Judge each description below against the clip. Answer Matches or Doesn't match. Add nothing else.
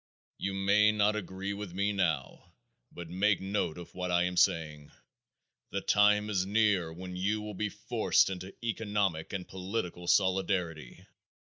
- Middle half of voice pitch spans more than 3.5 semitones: Doesn't match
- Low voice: Matches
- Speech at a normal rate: Matches